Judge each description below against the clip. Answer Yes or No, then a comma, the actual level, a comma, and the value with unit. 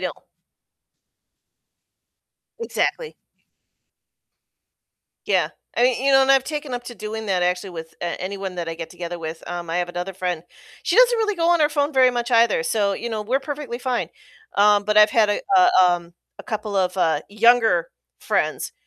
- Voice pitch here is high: Yes, high, 215 Hz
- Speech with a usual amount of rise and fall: No, wide, 6.7 semitones